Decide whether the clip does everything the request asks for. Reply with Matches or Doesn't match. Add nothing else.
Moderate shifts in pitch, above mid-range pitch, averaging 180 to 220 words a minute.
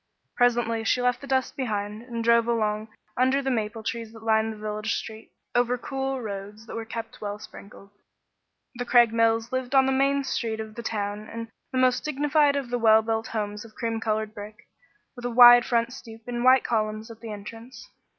Doesn't match